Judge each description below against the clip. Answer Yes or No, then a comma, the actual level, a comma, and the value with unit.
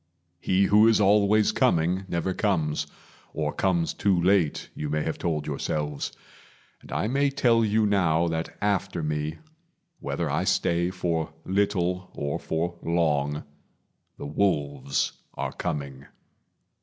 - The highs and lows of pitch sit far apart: No, average, 4.7 semitones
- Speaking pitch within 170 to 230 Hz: No, very low, 85 Hz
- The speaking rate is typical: No, slow, 130 wpm